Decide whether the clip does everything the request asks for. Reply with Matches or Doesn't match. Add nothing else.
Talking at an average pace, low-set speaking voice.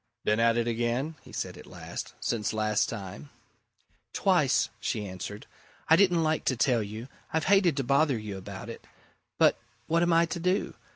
Matches